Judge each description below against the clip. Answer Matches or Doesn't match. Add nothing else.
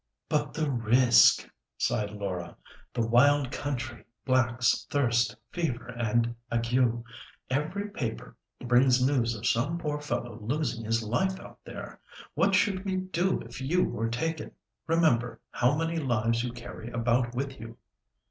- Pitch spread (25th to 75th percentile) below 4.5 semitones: Matches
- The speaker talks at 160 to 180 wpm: Doesn't match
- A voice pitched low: Matches